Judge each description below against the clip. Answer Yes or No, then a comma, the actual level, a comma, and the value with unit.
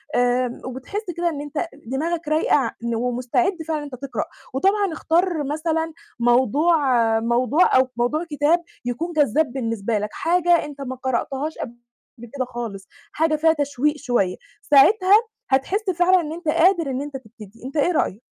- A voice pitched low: No, very high, 290 Hz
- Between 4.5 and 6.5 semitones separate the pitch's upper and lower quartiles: Yes, average, 5.0 semitones